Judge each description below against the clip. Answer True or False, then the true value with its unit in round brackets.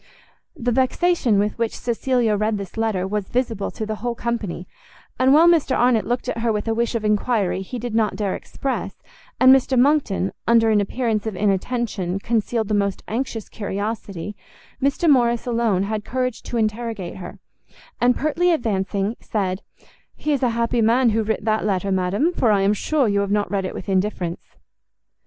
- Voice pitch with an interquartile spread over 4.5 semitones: False (3.3 semitones)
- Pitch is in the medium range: False (220 Hz)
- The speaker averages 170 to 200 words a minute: True (185 wpm)